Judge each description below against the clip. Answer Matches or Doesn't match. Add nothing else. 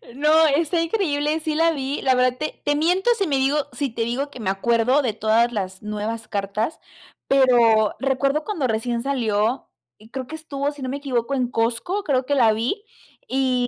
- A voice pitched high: Matches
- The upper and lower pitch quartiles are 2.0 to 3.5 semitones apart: Doesn't match